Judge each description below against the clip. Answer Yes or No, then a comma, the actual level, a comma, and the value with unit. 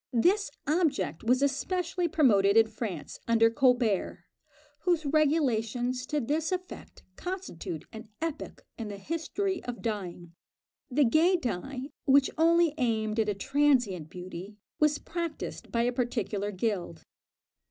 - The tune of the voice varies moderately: No, wide, 6.5 semitones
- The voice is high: Yes, very high, 250 Hz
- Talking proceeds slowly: Yes, slow, 130 wpm